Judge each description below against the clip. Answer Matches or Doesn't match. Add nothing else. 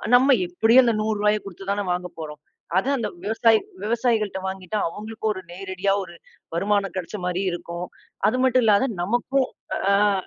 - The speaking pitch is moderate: Doesn't match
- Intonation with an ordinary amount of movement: Matches